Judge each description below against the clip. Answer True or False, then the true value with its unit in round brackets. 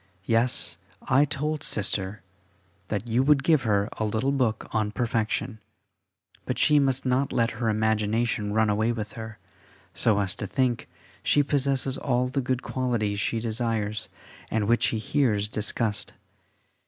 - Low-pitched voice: True (115 Hz)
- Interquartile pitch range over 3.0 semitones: True (3.4 semitones)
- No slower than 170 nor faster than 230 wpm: False (150 wpm)